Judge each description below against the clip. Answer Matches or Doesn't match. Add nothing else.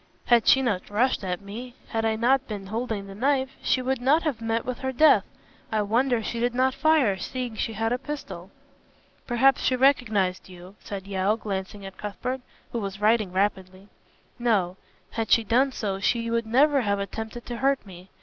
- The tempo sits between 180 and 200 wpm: Matches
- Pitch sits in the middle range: Doesn't match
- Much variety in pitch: Doesn't match